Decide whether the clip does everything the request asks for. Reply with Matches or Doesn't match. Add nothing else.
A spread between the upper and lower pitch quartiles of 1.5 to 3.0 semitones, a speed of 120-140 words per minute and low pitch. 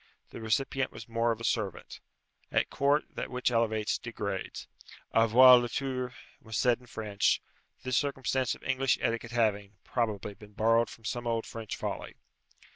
Doesn't match